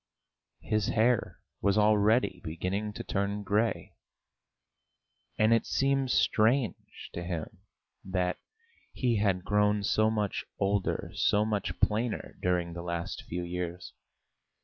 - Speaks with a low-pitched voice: Yes, low, 105 Hz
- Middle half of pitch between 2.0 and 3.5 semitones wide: Yes, average, 3.2 semitones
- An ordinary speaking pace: No, slow, 120 wpm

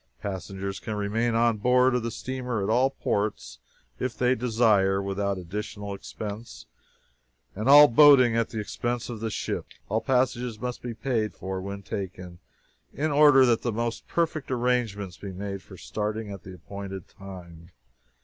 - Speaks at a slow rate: No, average, 160 wpm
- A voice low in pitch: Yes, low, 110 Hz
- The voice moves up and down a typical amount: Yes, average, 3.9 semitones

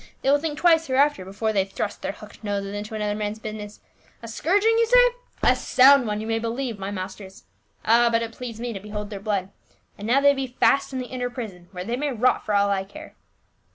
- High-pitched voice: Yes, high, 225 Hz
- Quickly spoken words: Yes, fast, 235 wpm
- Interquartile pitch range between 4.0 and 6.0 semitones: Yes, average, 4.5 semitones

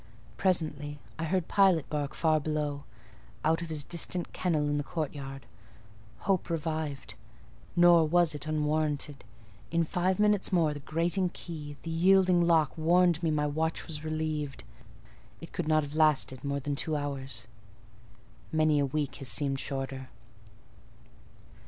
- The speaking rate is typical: Yes, average, 145 wpm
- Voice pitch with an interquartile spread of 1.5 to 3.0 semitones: Yes, narrow, 2.6 semitones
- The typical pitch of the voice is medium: Yes, medium, 155 Hz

